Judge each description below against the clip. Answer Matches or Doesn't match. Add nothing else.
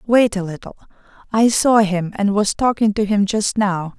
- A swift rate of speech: Doesn't match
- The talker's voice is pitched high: Matches